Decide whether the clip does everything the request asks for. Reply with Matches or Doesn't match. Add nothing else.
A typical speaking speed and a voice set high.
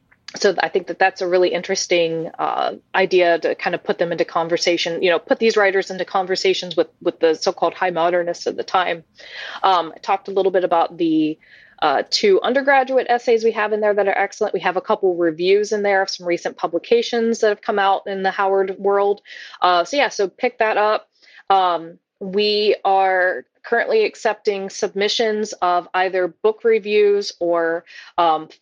Matches